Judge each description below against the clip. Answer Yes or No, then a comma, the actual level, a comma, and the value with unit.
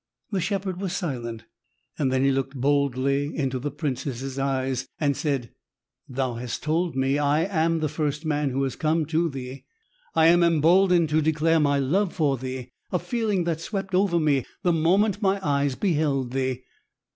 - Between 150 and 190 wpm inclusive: Yes, average, 170 wpm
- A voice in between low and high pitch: Yes, medium, 150 Hz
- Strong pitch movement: No, average, 4.1 semitones